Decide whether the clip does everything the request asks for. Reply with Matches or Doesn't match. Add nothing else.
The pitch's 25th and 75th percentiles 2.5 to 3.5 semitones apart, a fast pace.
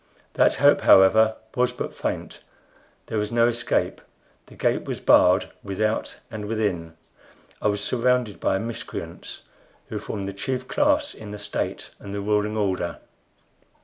Doesn't match